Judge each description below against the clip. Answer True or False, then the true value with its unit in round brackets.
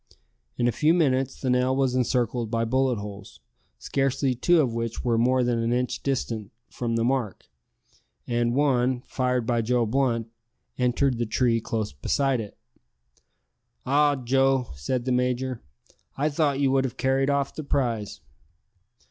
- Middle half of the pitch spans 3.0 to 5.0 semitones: False (2.5 semitones)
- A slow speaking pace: False (155 wpm)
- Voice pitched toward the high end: False (125 Hz)